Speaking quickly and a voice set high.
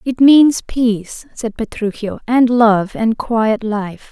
No: average, 145 wpm; high, 225 Hz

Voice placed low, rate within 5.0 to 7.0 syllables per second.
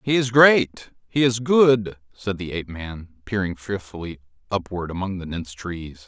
No: low, 100 Hz; 4.6 syllables/s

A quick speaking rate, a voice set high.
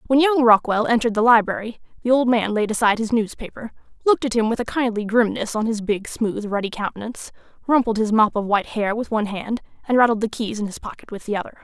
Yes: fast, 230 wpm; high, 225 Hz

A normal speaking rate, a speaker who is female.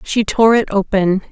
Yes: average, 180 wpm; female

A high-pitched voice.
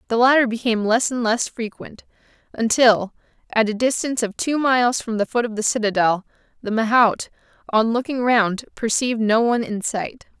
Yes: high, 230 Hz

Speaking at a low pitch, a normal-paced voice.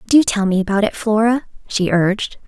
No: high, 210 Hz; average, 195 wpm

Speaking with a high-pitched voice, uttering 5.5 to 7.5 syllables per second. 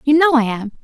Yes: very high, 265 Hz; 6.1 syllables/s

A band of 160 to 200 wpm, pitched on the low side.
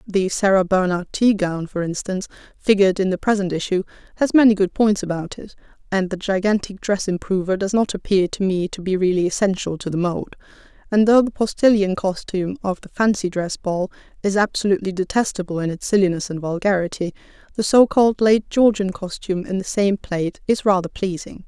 No: average, 180 wpm; high, 195 Hz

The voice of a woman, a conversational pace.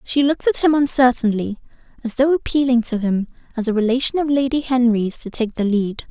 Yes: female; average, 195 wpm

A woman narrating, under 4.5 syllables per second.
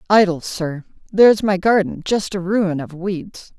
Yes: female; 4.3 syllables/s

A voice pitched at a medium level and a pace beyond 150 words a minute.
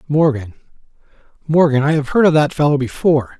No: medium, 145 Hz; average, 140 wpm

